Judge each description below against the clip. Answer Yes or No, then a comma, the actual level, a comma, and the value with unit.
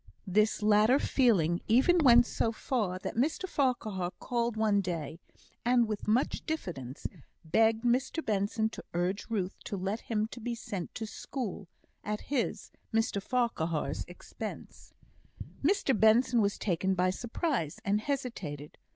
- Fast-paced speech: No, slow, 135 wpm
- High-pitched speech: Yes, high, 220 Hz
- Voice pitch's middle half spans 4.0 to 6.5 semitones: Yes, average, 4.4 semitones